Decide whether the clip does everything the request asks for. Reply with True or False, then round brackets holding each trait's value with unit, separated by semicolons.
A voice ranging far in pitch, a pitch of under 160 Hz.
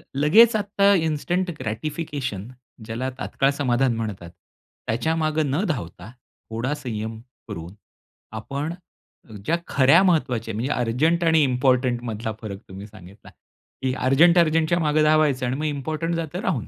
True (5.8 semitones; 135 Hz)